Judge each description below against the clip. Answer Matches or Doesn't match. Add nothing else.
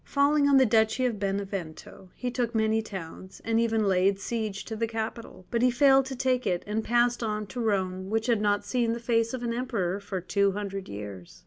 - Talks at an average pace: Doesn't match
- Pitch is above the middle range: Matches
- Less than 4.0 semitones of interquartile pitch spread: Matches